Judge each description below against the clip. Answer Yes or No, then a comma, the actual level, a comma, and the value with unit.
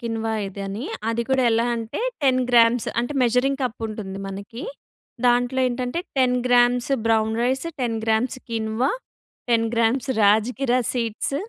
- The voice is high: Yes, high, 235 Hz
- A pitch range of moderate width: No, narrow, 2.1 semitones